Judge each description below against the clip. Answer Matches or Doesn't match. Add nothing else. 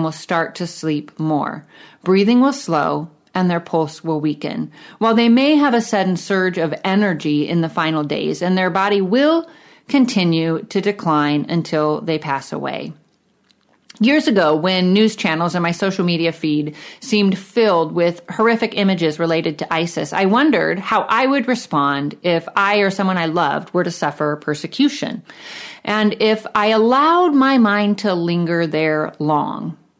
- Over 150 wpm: Matches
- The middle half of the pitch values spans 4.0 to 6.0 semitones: Matches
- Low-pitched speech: Doesn't match